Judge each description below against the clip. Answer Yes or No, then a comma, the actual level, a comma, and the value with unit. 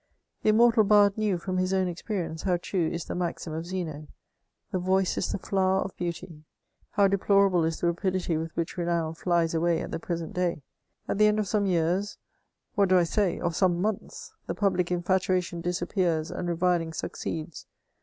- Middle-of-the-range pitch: Yes, medium, 180 Hz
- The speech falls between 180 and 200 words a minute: Yes, average, 190 wpm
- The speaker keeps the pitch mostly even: Yes, narrow, 2.3 semitones